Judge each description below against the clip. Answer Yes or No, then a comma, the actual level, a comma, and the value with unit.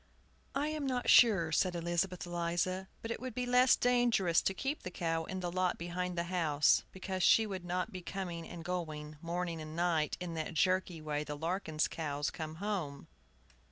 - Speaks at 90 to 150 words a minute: No, average, 190 wpm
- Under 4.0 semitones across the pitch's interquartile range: Yes, average, 2.7 semitones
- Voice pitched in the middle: Yes, medium, 175 Hz